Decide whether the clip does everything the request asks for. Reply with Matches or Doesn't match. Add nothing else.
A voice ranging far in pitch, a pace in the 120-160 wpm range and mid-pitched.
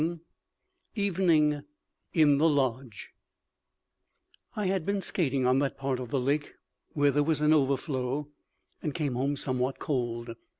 Doesn't match